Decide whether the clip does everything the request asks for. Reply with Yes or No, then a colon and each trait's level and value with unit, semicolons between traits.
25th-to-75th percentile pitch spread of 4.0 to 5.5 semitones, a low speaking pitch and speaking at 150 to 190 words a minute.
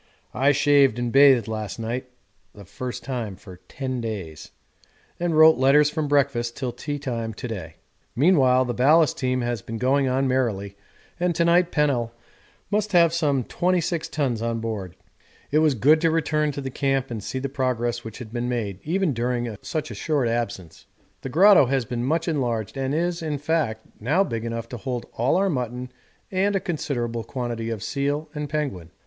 Yes: average, 4.4 semitones; low, 130 Hz; average, 185 wpm